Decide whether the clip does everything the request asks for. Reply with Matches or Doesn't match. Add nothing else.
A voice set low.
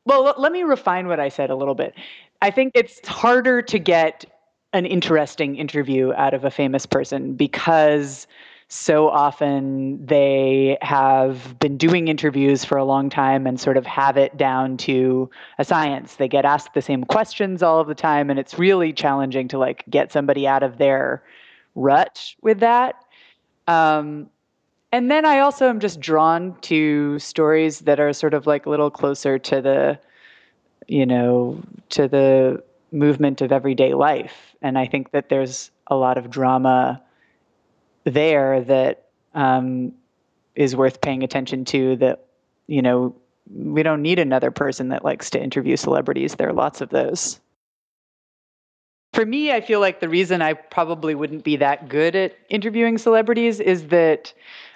Doesn't match